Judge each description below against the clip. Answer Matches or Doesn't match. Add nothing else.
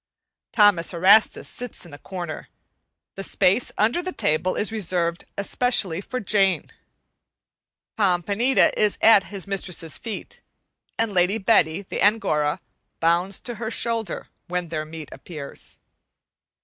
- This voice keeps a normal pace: Doesn't match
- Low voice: Doesn't match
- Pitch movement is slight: Doesn't match